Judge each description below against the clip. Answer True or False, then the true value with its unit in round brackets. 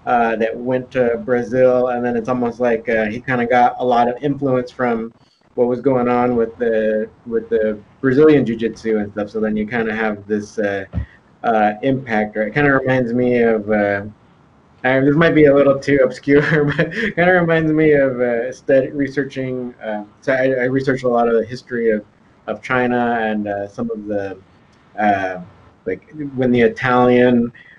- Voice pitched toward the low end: True (120 Hz)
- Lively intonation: False (3.4 semitones)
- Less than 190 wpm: False (200 wpm)